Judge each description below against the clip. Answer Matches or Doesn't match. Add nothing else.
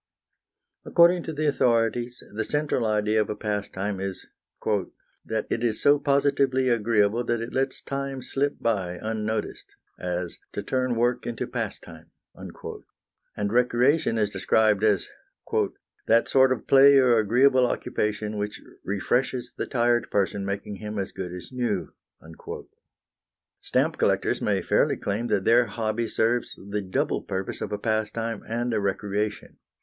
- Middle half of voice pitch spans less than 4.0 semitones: Matches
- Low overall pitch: Matches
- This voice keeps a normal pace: Matches